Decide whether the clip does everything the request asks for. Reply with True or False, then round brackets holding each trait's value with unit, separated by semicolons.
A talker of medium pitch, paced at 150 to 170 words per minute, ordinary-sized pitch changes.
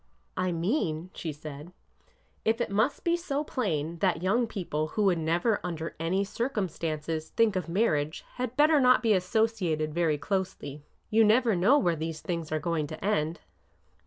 False (180 Hz; 165 wpm; 5.8 semitones)